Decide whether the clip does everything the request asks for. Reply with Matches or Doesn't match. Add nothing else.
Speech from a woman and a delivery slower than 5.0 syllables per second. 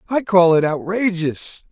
Doesn't match